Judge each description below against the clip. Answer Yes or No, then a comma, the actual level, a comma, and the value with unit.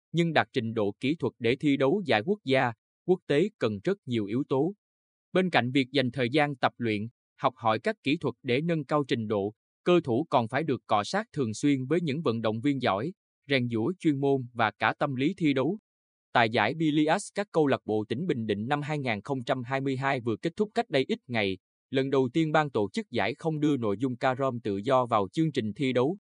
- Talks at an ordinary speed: Yes, average, 230 wpm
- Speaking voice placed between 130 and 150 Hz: Yes, low, 135 Hz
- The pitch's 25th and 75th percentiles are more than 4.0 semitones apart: Yes, average, 5.3 semitones